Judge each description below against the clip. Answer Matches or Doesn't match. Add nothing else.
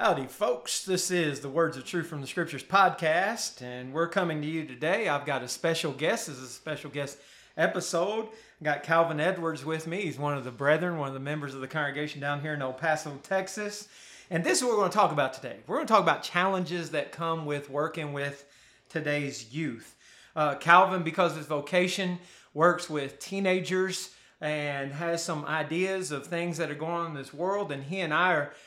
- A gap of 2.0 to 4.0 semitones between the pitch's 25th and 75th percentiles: Matches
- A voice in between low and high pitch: Matches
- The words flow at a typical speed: Doesn't match